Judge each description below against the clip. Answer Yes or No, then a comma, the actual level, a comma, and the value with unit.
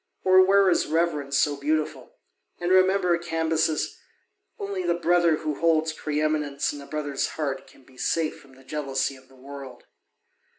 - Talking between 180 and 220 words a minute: No, average, 165 wpm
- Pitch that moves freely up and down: No, average, 3.5 semitones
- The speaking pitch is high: No, medium, 155 Hz